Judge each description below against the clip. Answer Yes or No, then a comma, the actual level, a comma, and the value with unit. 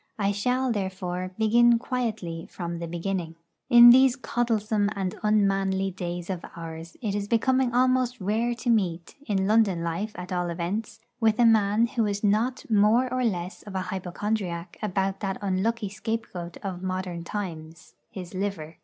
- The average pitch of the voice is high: Yes, high, 200 Hz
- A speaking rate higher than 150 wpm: Yes, average, 160 wpm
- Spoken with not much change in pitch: No, average, 3.9 semitones